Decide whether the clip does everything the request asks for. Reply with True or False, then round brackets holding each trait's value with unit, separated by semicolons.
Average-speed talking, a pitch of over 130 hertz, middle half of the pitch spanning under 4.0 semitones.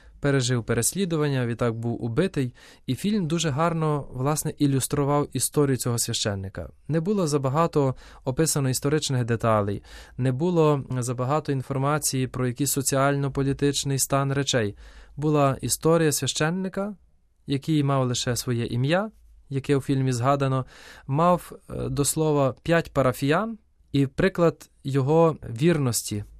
True (115 wpm; 140 Hz; 3.4 semitones)